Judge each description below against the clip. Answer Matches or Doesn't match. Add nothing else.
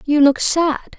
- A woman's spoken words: Matches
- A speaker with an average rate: Matches